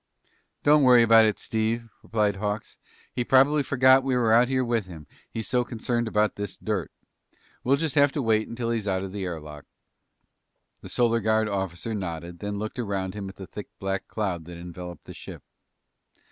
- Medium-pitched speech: No, low, 110 Hz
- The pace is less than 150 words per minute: No, average, 190 wpm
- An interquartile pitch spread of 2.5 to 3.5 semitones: No, average, 4.0 semitones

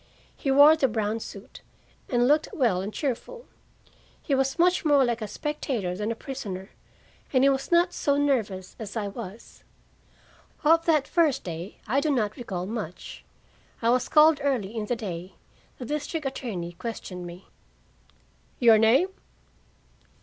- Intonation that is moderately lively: No, wide, 5.7 semitones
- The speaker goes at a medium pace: Yes, average, 155 wpm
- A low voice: No, high, 240 Hz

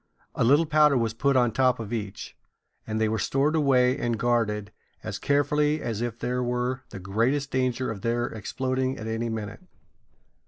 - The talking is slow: No, average, 180 wpm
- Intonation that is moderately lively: Yes, average, 3.1 semitones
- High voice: No, low, 120 Hz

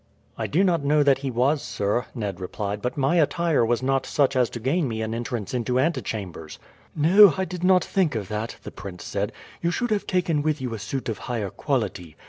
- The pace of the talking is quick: Yes, fast, 220 wpm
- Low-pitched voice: Yes, low, 130 Hz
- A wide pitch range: Yes, wide, 6.4 semitones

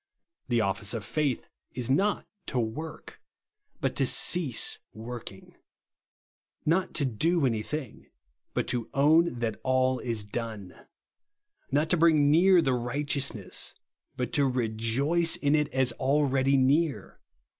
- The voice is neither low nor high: No, low, 130 Hz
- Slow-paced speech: Yes, slow, 130 wpm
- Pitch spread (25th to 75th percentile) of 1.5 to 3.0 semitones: No, average, 4.3 semitones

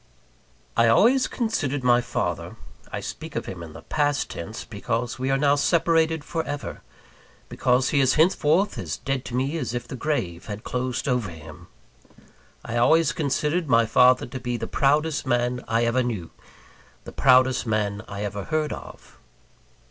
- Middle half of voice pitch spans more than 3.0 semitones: Yes, average, 4.2 semitones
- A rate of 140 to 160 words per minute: No, average, 170 wpm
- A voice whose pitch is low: Yes, low, 130 Hz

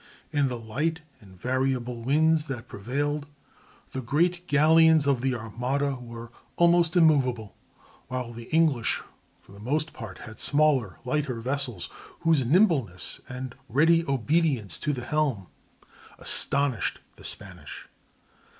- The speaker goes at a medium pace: No, slow, 125 wpm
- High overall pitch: No, low, 135 Hz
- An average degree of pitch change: Yes, average, 4.4 semitones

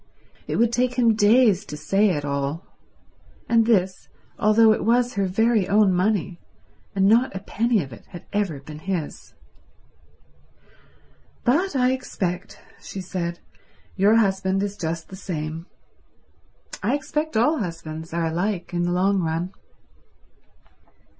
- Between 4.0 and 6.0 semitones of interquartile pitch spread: Yes, average, 4.7 semitones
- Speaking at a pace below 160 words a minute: Yes, average, 140 wpm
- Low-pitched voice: No, high, 195 Hz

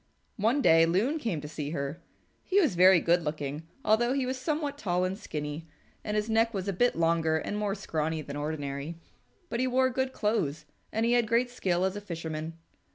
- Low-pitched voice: No, medium, 185 Hz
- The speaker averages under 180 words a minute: No, fast, 205 wpm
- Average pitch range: No, wide, 6.8 semitones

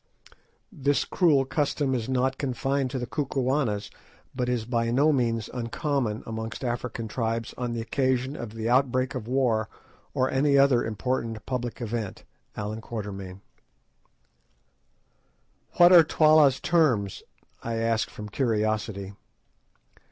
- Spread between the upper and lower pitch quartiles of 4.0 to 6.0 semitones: No, average, 3.2 semitones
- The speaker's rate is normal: No, slow, 120 wpm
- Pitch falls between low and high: No, low, 125 Hz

